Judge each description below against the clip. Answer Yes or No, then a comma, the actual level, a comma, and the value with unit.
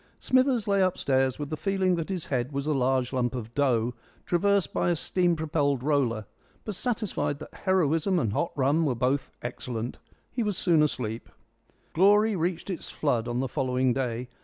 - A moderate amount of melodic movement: No, wide, 6.3 semitones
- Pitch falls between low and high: Yes, medium, 145 Hz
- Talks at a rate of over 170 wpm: Yes, average, 180 wpm